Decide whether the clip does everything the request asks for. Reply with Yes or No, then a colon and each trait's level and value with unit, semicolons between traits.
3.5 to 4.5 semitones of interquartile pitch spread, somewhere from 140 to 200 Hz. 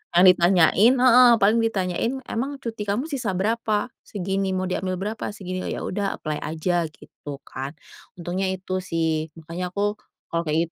Yes: average, 4.0 semitones; high, 190 Hz